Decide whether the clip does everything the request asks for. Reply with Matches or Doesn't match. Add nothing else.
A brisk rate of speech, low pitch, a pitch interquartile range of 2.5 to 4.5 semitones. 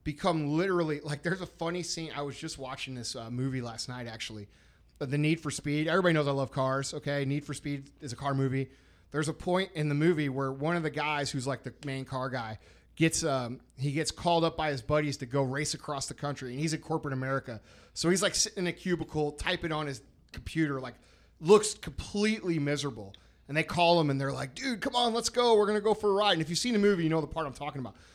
Doesn't match